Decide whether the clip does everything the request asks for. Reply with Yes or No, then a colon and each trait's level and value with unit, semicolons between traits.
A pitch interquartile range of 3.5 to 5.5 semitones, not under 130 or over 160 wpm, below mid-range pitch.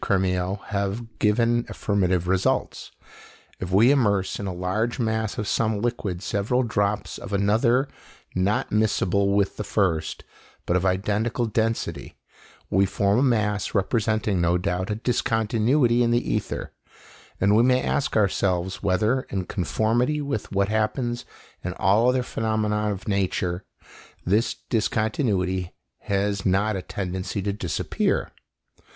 No: average, 3.0 semitones; slow, 135 wpm; low, 105 Hz